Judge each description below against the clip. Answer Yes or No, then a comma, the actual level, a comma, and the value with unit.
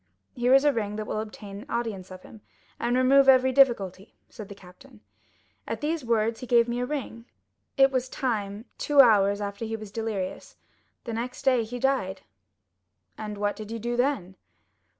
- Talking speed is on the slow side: No, average, 175 wpm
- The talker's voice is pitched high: Yes, high, 230 Hz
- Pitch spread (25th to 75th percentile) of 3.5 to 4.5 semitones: Yes, average, 3.8 semitones